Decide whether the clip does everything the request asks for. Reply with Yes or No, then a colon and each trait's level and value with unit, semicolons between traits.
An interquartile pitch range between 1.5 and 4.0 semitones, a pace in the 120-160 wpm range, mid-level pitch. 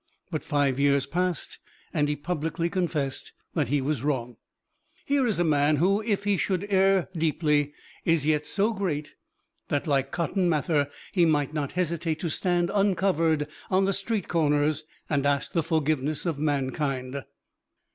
Yes: average, 3.7 semitones; average, 155 wpm; medium, 155 Hz